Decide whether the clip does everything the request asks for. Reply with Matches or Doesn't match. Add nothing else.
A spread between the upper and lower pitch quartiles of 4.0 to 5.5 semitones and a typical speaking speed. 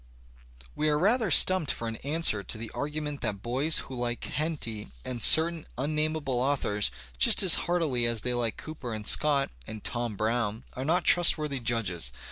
Matches